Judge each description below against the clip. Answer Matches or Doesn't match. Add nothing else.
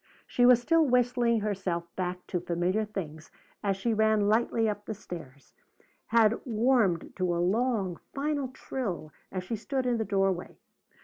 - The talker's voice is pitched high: Matches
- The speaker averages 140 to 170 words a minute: Matches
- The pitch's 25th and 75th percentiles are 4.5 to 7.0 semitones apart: Matches